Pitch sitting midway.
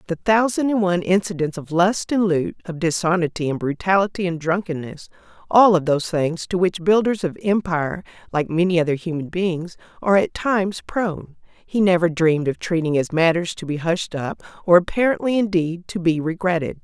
Yes: medium, 175 Hz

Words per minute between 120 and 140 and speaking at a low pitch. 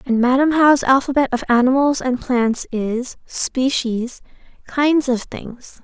No: slow, 135 wpm; very high, 255 Hz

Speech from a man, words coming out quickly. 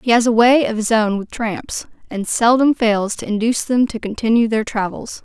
No: female; fast, 220 wpm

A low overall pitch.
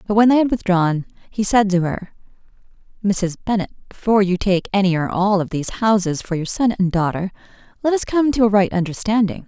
No: high, 200 Hz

